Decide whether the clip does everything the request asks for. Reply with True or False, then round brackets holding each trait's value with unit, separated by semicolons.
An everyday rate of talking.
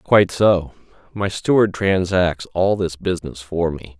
True (150 wpm)